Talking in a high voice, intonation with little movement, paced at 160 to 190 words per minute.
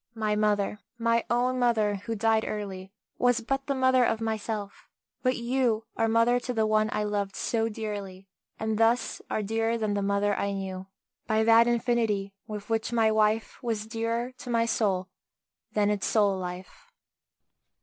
Yes: high, 220 Hz; narrow, 2.1 semitones; average, 170 wpm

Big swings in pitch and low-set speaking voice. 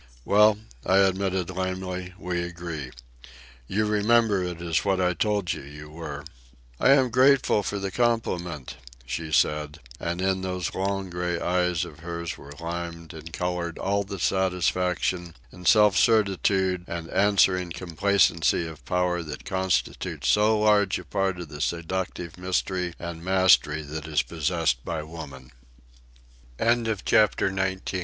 No: average, 2.7 semitones; very low, 90 Hz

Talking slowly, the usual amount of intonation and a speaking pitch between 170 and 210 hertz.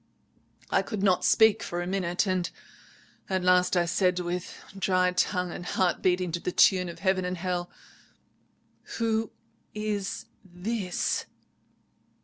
No: slow, 130 wpm; narrow, 1.6 semitones; medium, 185 Hz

